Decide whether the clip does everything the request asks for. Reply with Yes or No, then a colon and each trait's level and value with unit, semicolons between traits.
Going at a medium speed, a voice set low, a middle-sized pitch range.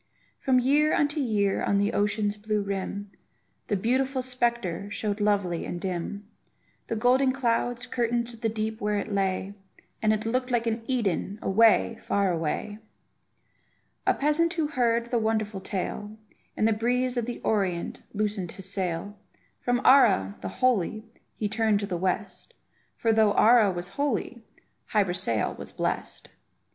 No: average, 155 wpm; high, 215 Hz; average, 3.3 semitones